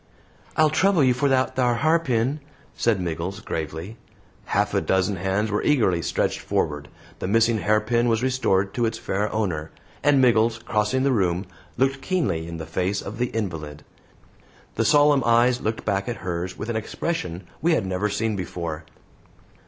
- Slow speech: No, average, 170 wpm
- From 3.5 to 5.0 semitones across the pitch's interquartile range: No, wide, 5.4 semitones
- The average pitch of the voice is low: Yes, low, 110 Hz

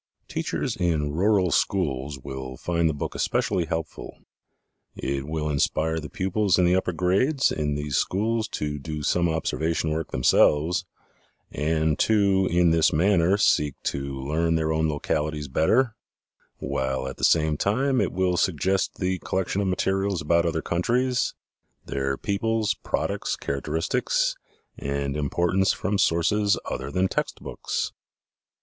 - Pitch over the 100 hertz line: No, very low, 80 Hz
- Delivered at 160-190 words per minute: No, average, 140 wpm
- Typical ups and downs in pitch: Yes, average, 4.4 semitones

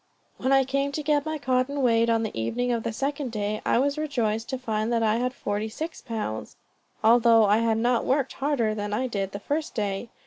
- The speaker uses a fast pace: Yes, fast, 220 wpm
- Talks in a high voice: Yes, high, 235 Hz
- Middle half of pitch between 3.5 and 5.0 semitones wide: Yes, average, 3.9 semitones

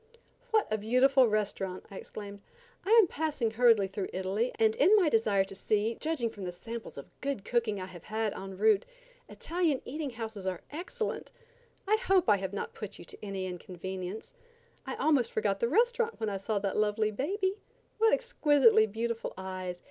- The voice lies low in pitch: No, high, 220 Hz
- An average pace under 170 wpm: No, average, 180 wpm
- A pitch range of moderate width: No, wide, 6.9 semitones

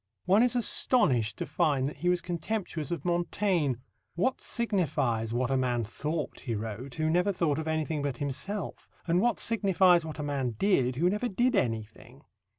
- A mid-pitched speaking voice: Yes, medium, 160 Hz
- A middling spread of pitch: No, wide, 6.3 semitones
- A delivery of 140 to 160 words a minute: No, average, 175 wpm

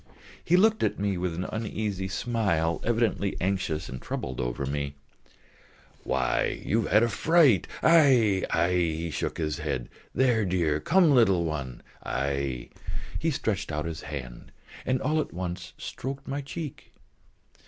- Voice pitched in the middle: No, very low, 95 Hz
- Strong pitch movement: Yes, wide, 7.5 semitones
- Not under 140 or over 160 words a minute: Yes, average, 150 wpm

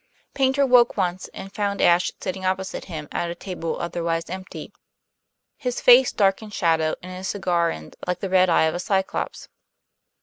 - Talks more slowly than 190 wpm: Yes, average, 175 wpm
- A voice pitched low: No, medium, 185 Hz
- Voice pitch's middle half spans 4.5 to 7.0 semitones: No, average, 2.7 semitones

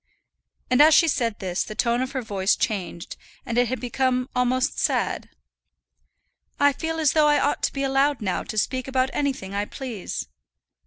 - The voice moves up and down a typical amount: Yes, average, 4.1 semitones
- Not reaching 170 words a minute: No, average, 190 wpm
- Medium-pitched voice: No, very high, 255 Hz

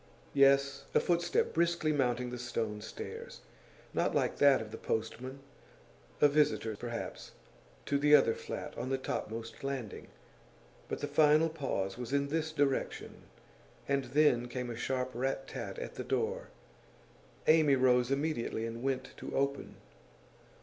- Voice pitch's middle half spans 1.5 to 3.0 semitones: No, average, 3.4 semitones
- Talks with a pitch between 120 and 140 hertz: Yes, low, 135 Hz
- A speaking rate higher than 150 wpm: No, average, 145 wpm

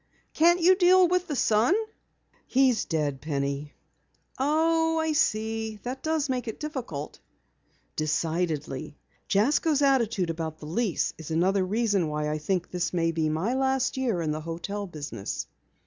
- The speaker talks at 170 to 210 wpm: No, average, 150 wpm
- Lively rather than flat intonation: Yes, wide, 9.0 semitones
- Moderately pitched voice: No, high, 205 Hz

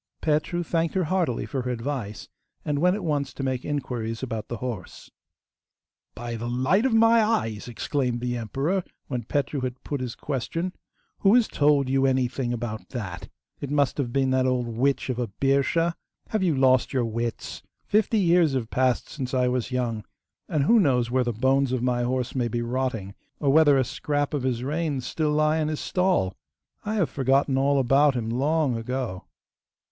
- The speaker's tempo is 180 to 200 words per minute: Yes, average, 190 wpm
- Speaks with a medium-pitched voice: No, low, 130 Hz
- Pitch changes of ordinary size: Yes, average, 3.7 semitones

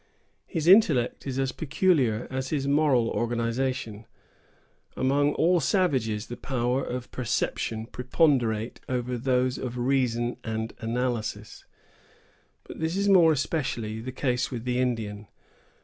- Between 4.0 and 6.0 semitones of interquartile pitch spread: No, average, 3.1 semitones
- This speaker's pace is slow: Yes, slow, 125 wpm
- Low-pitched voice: Yes, low, 125 Hz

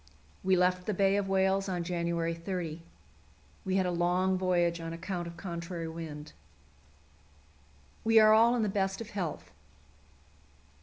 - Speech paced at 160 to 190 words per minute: No, average, 150 wpm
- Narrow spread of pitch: Yes, narrow, 2.3 semitones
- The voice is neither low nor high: Yes, medium, 180 Hz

